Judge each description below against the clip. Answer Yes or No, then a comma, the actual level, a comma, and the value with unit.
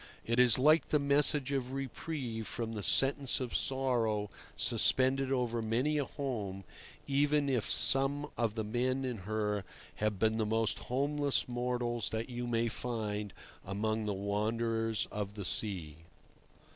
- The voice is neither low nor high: No, low, 120 Hz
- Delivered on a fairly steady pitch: No, average, 3.7 semitones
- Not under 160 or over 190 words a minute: No, average, 145 wpm